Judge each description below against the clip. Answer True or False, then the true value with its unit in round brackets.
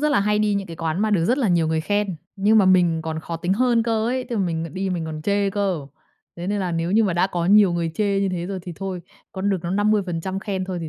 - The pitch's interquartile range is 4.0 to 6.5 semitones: False (3.2 semitones)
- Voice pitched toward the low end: False (190 Hz)